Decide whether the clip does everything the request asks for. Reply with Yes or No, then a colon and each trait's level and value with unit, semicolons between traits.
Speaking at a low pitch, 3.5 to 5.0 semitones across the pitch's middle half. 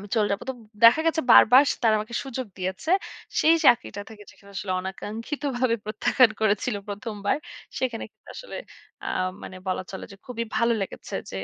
No: high, 230 Hz; average, 3.9 semitones